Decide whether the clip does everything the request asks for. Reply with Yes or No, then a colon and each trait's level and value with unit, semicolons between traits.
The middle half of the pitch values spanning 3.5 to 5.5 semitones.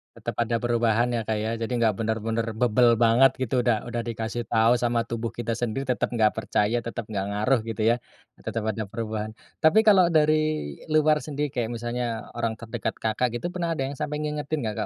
No: average, 2.9 semitones